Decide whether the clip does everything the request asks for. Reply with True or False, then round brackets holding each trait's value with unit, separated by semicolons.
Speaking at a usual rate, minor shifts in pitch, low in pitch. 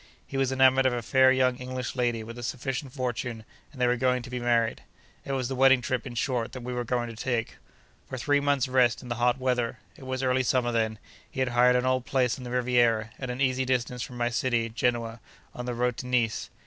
False (245 wpm; 1.4 semitones; 125 Hz)